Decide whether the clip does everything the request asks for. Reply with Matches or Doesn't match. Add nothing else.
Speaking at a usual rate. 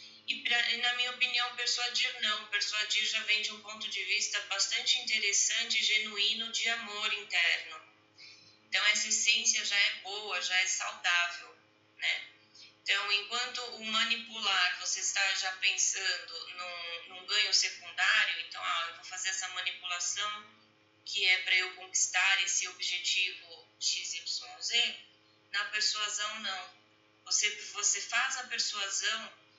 Matches